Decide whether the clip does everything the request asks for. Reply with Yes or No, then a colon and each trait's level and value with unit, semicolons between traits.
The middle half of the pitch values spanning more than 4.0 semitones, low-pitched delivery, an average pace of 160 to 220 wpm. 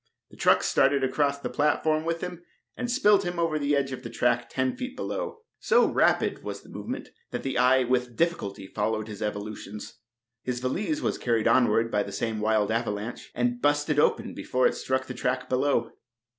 Yes: average, 5.1 semitones; low, 130 Hz; average, 190 wpm